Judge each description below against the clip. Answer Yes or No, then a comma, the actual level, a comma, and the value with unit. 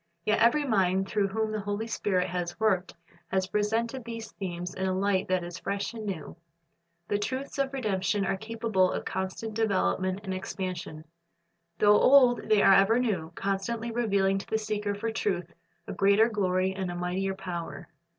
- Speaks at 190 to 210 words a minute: No, average, 175 wpm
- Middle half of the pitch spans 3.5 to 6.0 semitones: No, average, 2.9 semitones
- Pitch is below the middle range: No, high, 200 Hz